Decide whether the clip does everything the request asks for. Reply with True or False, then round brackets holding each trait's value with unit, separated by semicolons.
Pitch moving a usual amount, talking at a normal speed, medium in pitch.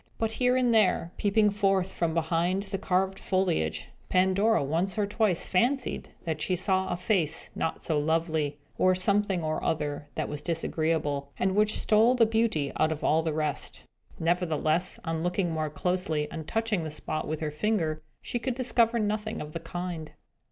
True (4.8 semitones; 175 wpm; 180 Hz)